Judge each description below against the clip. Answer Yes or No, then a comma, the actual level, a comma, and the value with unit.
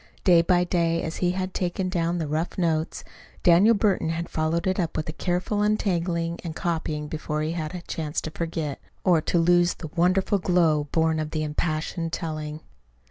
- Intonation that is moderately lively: No, narrow, 2.1 semitones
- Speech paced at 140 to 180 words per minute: No, average, 190 wpm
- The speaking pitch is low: No, medium, 170 Hz